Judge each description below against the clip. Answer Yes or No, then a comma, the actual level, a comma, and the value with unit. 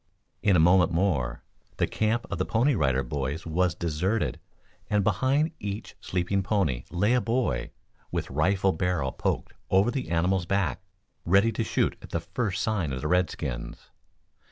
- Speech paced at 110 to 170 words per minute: Yes, average, 160 wpm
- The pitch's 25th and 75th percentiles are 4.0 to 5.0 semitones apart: Yes, average, 4.6 semitones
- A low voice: Yes, very low, 95 Hz